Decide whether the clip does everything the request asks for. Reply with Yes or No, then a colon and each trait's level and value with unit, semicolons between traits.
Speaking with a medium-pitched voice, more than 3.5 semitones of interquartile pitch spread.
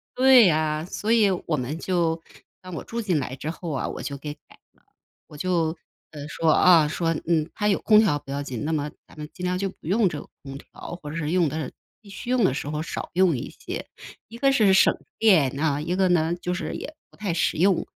Yes: medium, 165 Hz; average, 4.1 semitones